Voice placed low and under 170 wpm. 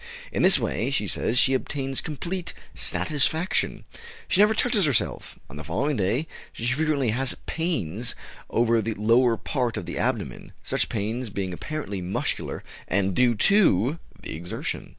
Yes: low, 125 Hz; average, 150 wpm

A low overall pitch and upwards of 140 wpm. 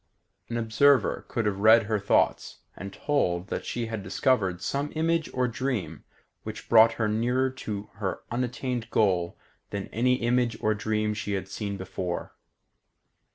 Yes: low, 110 Hz; average, 155 wpm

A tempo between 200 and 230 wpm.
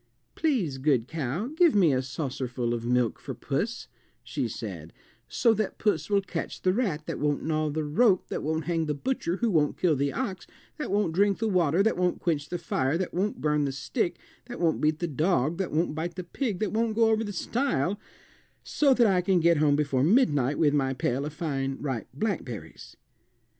Yes: fast, 205 wpm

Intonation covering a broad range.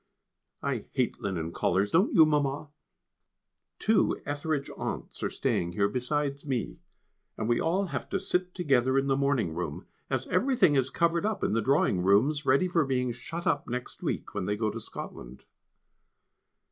Yes: wide, 6.4 semitones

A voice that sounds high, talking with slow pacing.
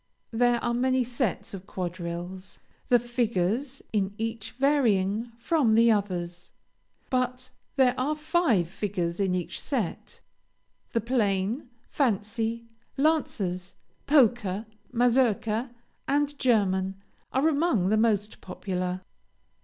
Yes: high, 225 Hz; slow, 105 wpm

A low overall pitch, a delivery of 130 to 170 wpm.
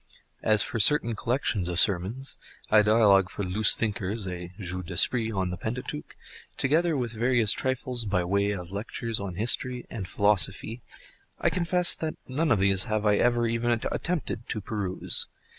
Yes: low, 110 Hz; average, 160 wpm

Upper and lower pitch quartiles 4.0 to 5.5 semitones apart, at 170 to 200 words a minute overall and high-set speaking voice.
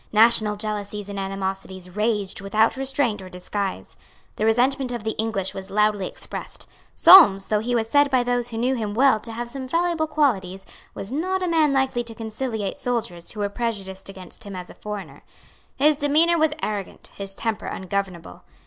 Yes: average, 4.9 semitones; average, 180 wpm; high, 220 Hz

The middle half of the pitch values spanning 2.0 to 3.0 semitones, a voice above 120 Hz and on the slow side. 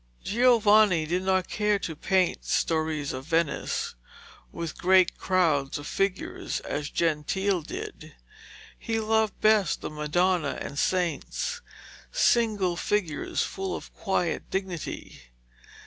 No: average, 4.3 semitones; medium, 185 Hz; slow, 115 wpm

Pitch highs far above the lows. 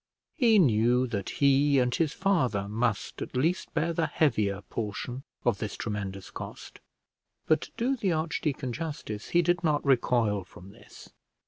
Yes: wide, 7.2 semitones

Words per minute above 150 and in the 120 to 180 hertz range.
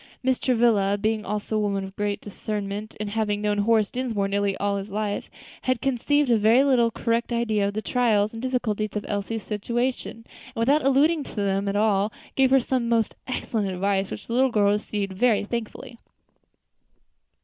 No: average, 180 wpm; high, 215 Hz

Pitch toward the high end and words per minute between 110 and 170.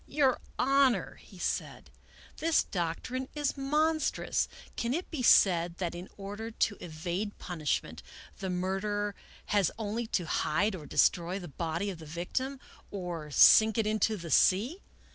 Yes: high, 205 Hz; average, 160 wpm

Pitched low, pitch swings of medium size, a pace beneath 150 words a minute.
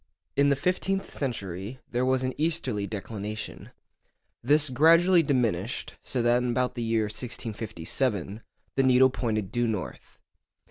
Yes: low, 120 Hz; average, 4.1 semitones; slow, 135 wpm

